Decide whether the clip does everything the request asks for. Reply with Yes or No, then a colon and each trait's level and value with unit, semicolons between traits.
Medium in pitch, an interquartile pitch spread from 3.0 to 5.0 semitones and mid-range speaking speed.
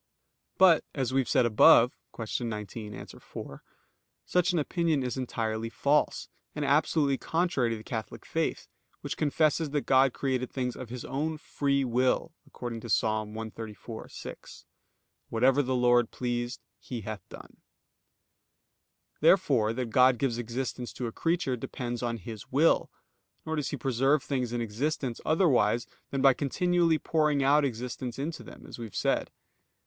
No: low, 130 Hz; average, 3.7 semitones; average, 155 wpm